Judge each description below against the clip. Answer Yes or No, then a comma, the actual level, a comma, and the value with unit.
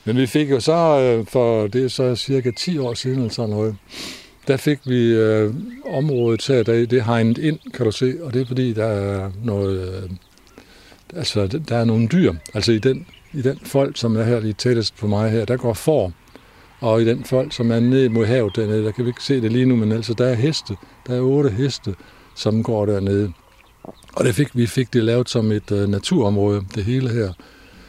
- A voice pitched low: Yes, low, 120 Hz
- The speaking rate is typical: Yes, average, 215 wpm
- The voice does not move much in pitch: No, average, 3.2 semitones